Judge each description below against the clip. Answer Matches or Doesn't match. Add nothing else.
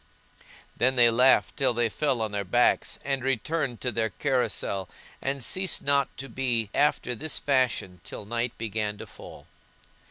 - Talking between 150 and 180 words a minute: Matches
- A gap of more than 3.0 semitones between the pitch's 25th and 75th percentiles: Matches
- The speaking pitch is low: Matches